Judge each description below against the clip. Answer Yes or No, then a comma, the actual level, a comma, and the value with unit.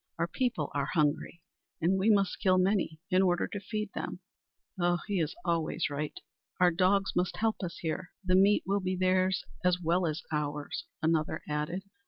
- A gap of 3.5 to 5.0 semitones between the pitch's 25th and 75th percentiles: No, average, 2.9 semitones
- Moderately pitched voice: Yes, medium, 180 Hz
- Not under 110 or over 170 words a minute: No, average, 180 wpm